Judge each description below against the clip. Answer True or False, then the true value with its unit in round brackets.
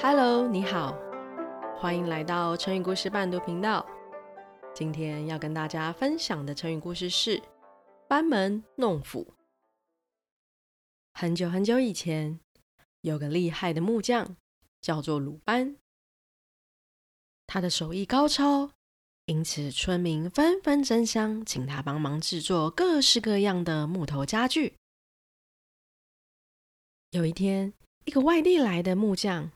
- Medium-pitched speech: True (175 Hz)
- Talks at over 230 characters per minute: False (190 characters per minute)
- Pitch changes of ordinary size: False (6.1 semitones)